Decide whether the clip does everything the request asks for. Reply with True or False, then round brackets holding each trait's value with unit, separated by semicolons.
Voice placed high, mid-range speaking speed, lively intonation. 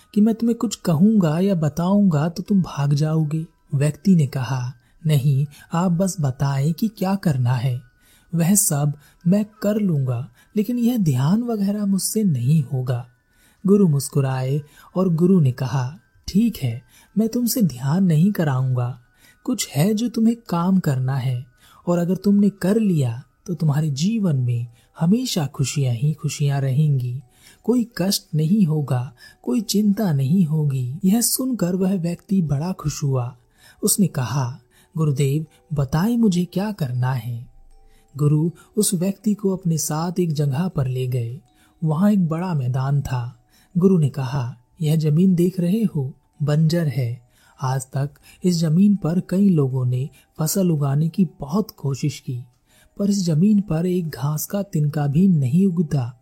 False (155 Hz; 150 wpm; 6.0 semitones)